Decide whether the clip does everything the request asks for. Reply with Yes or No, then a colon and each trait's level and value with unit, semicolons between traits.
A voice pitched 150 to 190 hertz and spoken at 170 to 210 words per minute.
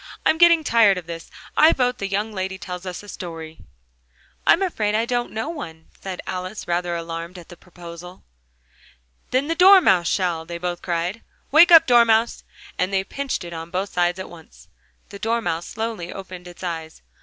Yes: medium, 185 Hz; average, 180 wpm